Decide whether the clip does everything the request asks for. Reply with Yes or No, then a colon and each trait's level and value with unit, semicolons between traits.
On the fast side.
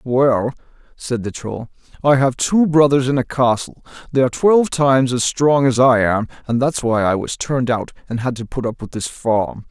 Yes: fast, 215 wpm